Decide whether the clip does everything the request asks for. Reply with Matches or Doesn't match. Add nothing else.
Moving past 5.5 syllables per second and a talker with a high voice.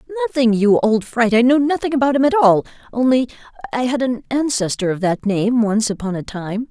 Matches